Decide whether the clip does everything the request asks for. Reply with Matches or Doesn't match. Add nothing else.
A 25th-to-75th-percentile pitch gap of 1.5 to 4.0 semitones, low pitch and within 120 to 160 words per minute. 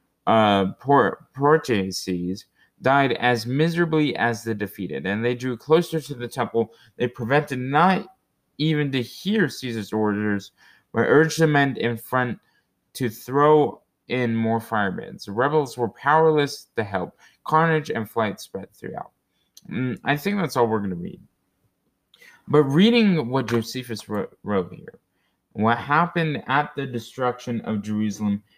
Doesn't match